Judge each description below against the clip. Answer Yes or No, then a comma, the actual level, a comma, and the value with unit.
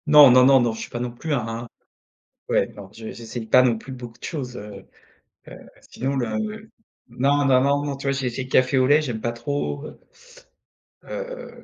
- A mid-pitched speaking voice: No, low, 130 Hz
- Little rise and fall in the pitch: No, average, 3.2 semitones